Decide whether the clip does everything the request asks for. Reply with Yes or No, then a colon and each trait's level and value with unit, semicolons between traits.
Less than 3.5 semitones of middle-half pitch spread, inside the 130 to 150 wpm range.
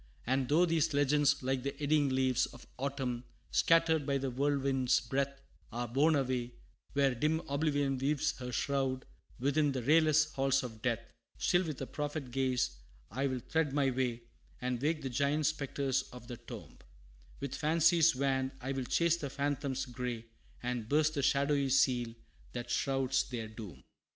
No: narrow, 2.5 semitones; average, 160 wpm